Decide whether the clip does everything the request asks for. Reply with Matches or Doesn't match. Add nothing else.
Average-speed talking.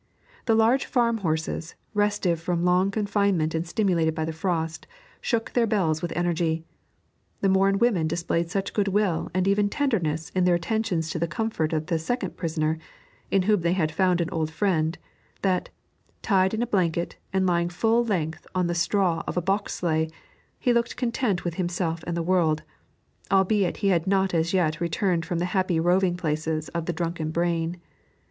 Matches